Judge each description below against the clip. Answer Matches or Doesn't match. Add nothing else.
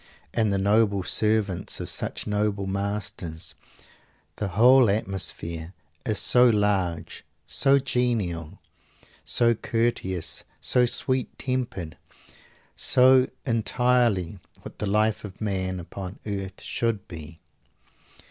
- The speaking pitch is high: Doesn't match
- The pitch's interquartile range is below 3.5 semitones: Doesn't match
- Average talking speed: Doesn't match